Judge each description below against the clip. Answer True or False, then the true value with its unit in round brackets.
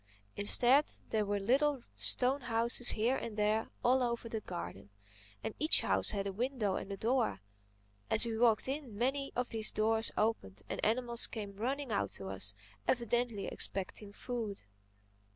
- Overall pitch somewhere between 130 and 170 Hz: False (225 Hz)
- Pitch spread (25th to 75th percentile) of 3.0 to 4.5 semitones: True (3.4 semitones)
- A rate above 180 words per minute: False (160 wpm)